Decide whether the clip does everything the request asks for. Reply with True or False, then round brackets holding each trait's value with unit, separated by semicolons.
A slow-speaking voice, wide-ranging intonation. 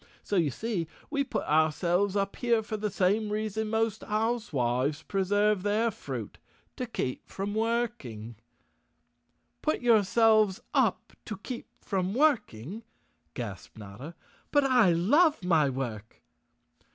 True (125 wpm; 6.1 semitones)